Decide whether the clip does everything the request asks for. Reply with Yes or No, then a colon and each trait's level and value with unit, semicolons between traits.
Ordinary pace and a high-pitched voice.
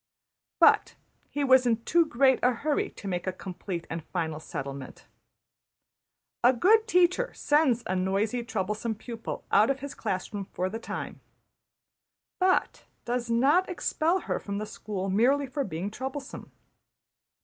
Yes: average, 150 wpm; high, 235 Hz